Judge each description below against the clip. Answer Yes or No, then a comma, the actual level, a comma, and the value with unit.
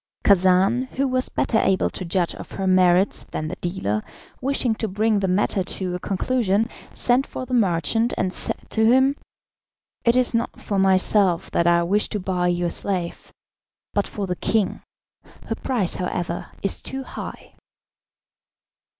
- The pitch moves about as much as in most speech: Yes, average, 4.2 semitones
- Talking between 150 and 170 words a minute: Yes, average, 160 wpm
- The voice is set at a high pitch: Yes, high, 195 Hz